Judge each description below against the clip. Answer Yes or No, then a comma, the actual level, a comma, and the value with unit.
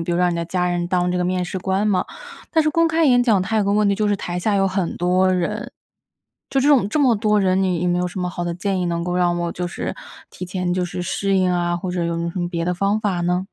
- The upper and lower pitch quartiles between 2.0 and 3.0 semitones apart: Yes, narrow, 2.4 semitones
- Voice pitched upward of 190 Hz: No, medium, 185 Hz